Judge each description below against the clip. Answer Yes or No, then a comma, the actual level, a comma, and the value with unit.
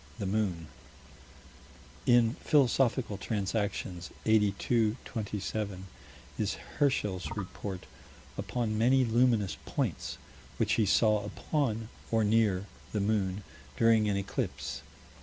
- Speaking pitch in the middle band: No, low, 110 Hz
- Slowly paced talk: Yes, slow, 100 wpm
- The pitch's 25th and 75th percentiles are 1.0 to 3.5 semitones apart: Yes, narrow, 2.5 semitones